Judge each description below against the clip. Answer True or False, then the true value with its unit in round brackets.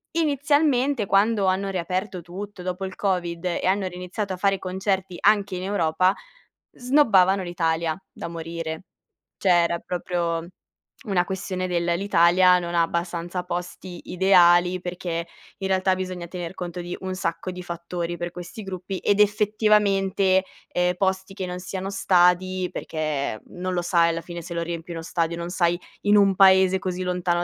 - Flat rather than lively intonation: True (1.9 semitones)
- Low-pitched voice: False (180 Hz)